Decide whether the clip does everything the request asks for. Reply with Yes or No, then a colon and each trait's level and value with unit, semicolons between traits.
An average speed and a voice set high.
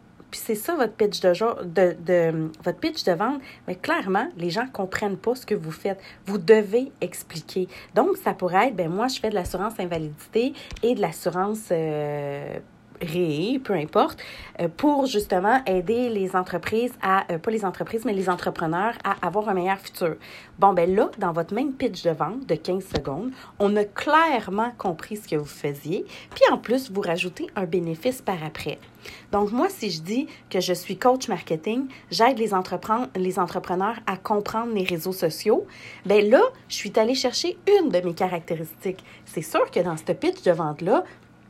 Yes: average, 185 wpm; high, 195 Hz